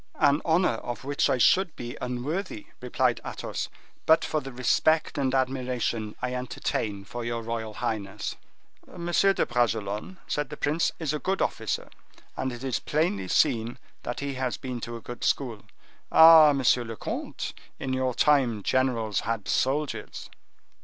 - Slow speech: No, average, 160 wpm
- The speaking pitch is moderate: No, low, 125 Hz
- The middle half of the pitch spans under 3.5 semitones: No, average, 4.1 semitones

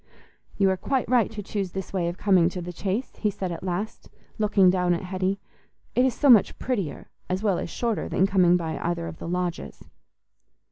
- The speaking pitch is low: No, high, 190 Hz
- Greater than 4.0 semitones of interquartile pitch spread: No, average, 3.0 semitones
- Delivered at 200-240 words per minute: Yes, fast, 205 wpm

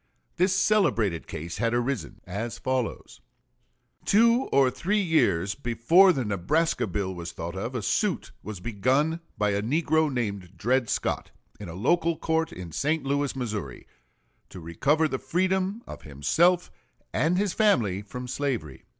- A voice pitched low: Yes, low, 125 Hz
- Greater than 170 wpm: No, average, 150 wpm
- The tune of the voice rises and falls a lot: Yes, wide, 8.4 semitones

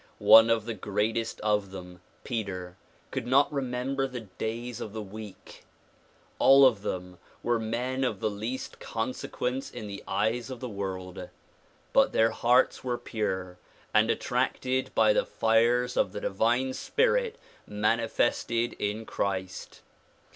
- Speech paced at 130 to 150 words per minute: Yes, average, 140 wpm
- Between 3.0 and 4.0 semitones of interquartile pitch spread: Yes, average, 3.5 semitones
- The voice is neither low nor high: No, low, 115 Hz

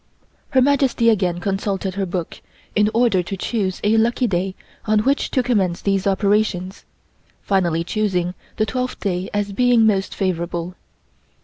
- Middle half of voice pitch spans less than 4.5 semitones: Yes, average, 3.3 semitones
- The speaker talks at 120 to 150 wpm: Yes, average, 145 wpm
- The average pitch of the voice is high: Yes, high, 200 Hz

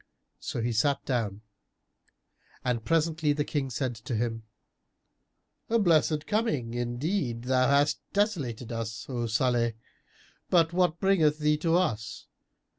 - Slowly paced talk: Yes, slow, 125 wpm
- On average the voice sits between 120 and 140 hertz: Yes, low, 135 Hz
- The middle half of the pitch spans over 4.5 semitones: Yes, wide, 5.6 semitones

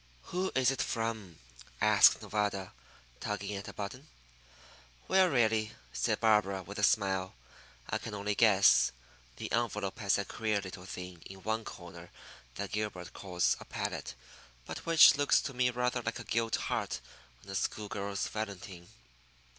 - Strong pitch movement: No, average, 3.0 semitones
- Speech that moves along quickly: No, average, 155 wpm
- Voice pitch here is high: No, low, 105 Hz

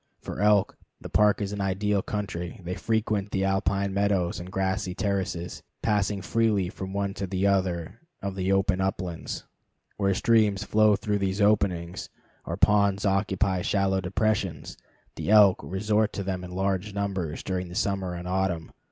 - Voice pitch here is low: Yes, very low, 95 Hz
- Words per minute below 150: No, average, 160 wpm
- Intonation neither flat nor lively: No, narrow, 1.7 semitones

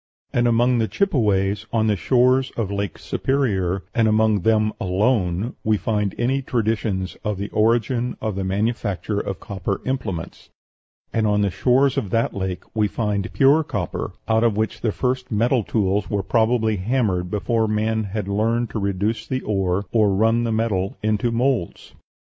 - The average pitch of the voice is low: Yes, low, 110 Hz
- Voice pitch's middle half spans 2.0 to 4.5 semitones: Yes, average, 2.9 semitones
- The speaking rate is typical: Yes, average, 165 wpm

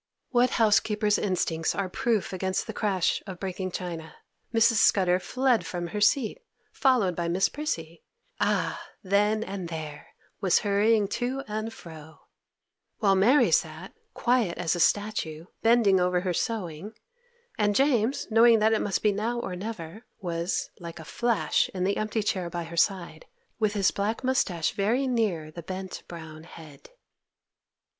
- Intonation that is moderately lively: Yes, average, 4.4 semitones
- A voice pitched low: No, high, 195 Hz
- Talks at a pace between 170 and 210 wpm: No, average, 155 wpm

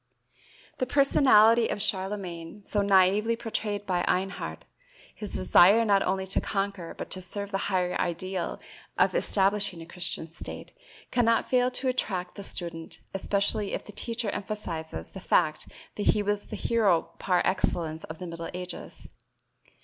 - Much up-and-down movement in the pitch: No, average, 2.9 semitones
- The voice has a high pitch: Yes, high, 195 Hz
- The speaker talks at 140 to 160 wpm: Yes, average, 150 wpm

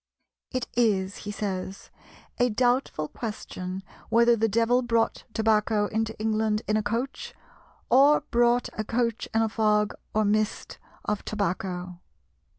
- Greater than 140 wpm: No, slow, 135 wpm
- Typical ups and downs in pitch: No, narrow, 2.2 semitones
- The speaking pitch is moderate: No, high, 220 Hz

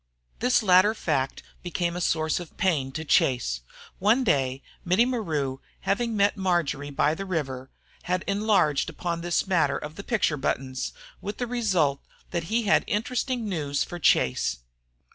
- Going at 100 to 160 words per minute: Yes, average, 155 wpm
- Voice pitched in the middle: Yes, medium, 175 Hz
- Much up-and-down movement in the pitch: Yes, wide, 6.2 semitones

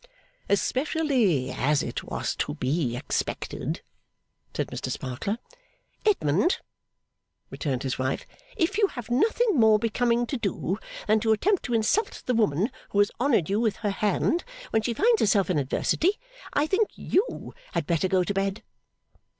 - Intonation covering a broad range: Yes, wide, 7.7 semitones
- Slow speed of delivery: No, average, 155 wpm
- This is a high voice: Yes, high, 220 Hz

